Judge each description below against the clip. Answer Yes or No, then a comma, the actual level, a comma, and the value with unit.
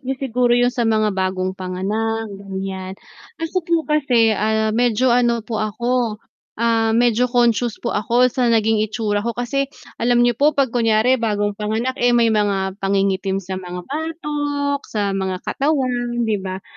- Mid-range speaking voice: No, high, 225 Hz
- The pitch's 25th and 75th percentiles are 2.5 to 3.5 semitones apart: Yes, average, 3.2 semitones